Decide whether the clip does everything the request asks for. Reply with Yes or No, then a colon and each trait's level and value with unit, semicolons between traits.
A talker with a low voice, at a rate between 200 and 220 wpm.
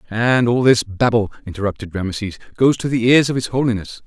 No: low, 115 Hz; average, 190 wpm